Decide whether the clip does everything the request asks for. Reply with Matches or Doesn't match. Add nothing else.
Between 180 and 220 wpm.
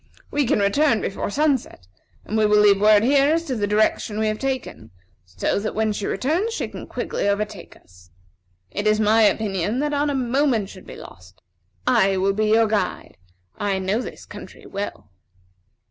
Matches